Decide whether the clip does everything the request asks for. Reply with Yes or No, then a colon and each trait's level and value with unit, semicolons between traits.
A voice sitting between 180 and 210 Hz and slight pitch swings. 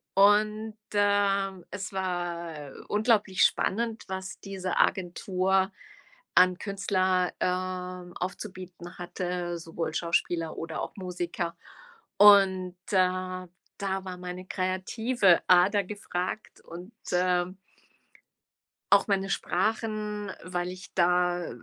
Yes: medium, 185 Hz; narrow, 1.9 semitones